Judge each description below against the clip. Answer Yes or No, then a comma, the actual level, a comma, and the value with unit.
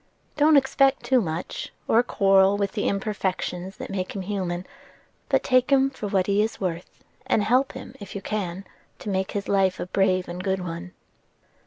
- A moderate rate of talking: Yes, average, 185 wpm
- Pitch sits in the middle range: No, high, 195 Hz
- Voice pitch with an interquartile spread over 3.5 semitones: No, average, 2.7 semitones